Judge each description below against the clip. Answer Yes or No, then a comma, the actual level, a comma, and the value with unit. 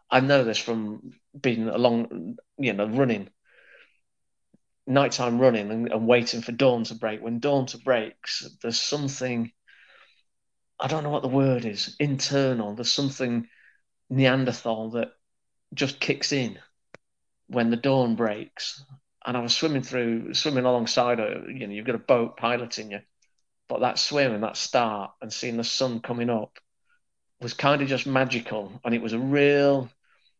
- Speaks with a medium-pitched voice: No, low, 120 Hz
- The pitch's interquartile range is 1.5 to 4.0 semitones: Yes, narrow, 2.6 semitones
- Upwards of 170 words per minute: No, average, 160 wpm